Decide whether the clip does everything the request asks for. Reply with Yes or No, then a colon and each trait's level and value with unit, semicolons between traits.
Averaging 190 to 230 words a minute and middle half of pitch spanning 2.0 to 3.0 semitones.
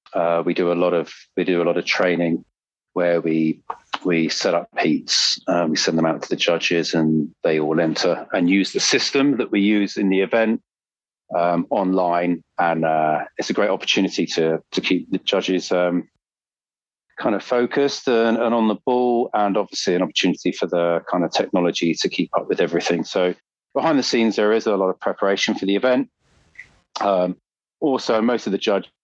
No: average, 195 wpm; average, 4.2 semitones